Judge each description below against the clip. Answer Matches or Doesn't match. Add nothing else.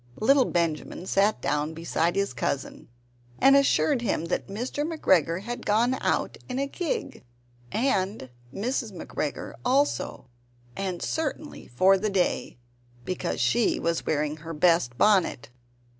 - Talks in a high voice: Matches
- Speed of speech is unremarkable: Doesn't match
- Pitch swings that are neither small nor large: Doesn't match